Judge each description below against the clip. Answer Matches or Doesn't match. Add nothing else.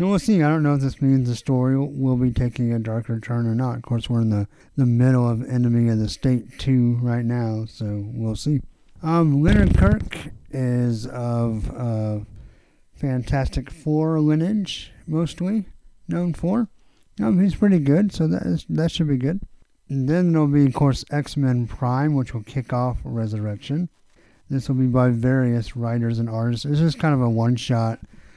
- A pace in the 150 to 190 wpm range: Matches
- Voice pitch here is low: Matches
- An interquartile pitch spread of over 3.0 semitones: Matches